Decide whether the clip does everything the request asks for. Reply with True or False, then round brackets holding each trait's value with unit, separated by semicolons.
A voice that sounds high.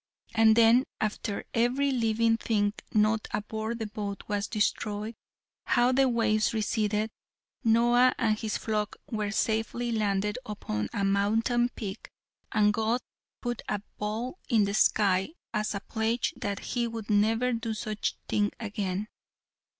True (220 Hz)